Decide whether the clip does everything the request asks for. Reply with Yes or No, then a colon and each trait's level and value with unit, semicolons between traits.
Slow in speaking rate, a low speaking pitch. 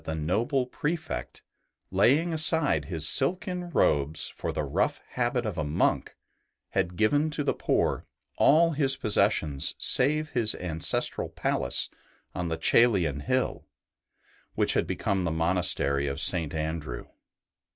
Yes: slow, 130 wpm; low, 100 Hz